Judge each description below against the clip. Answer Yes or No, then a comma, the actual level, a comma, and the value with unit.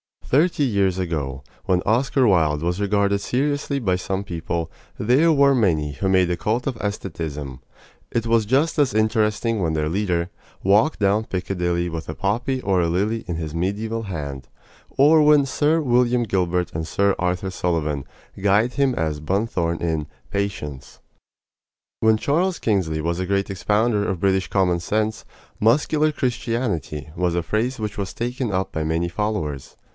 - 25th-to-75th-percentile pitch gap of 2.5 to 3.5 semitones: No, average, 5.3 semitones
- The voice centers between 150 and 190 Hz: No, low, 100 Hz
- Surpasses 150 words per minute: Yes, average, 160 wpm